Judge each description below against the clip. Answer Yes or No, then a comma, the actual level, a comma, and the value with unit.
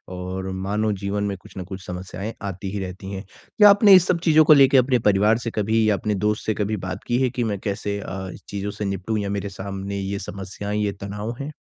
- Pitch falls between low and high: No, low, 100 Hz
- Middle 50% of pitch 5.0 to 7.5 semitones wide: No, narrow, 2.4 semitones